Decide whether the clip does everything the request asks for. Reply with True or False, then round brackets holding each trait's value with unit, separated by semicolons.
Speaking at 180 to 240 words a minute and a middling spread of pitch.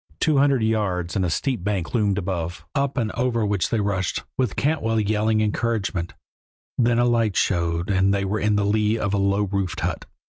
True (195 wpm; 3.2 semitones)